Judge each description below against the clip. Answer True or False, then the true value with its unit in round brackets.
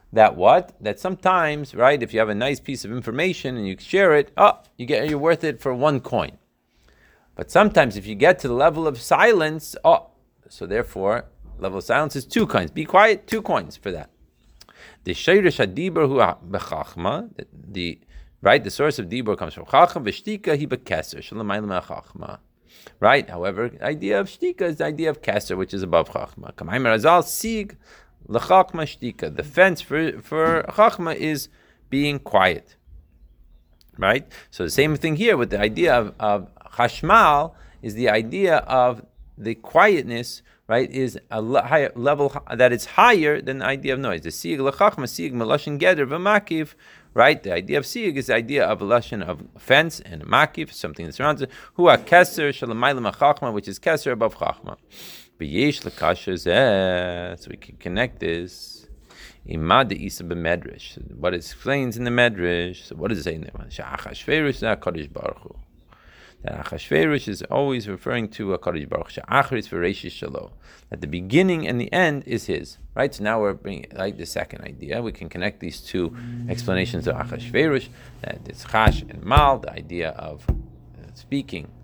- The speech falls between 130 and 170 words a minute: True (155 wpm)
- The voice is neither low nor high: False (130 Hz)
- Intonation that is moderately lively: False (7.5 semitones)